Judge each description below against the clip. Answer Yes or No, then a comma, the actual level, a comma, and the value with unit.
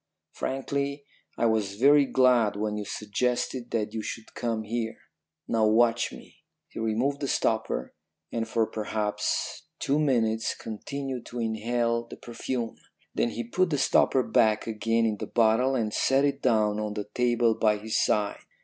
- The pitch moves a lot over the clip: No, narrow, 2.6 semitones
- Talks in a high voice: No, low, 115 Hz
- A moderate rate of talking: Yes, average, 160 wpm